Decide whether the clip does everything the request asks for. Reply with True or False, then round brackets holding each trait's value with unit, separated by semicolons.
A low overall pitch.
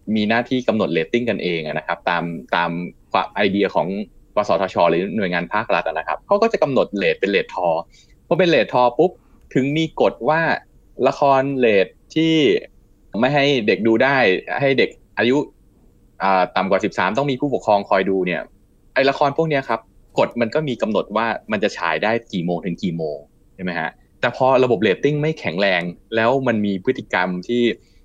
True (120 Hz)